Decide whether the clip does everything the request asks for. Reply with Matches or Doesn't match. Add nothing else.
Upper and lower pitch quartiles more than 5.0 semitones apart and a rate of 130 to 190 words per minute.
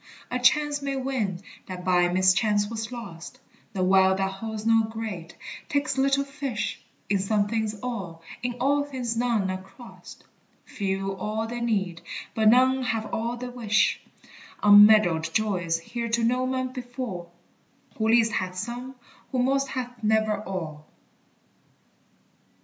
Doesn't match